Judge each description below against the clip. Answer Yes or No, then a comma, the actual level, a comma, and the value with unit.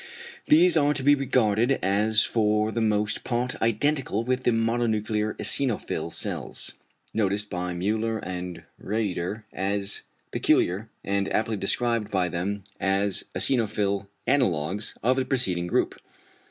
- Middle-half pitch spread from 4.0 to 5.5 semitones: No, average, 3.3 semitones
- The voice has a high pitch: No, low, 105 Hz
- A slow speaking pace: Yes, slow, 130 wpm